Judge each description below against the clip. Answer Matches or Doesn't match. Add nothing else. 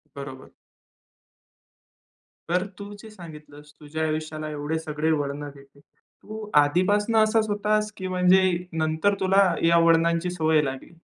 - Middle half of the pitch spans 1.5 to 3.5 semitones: Doesn't match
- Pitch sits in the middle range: Matches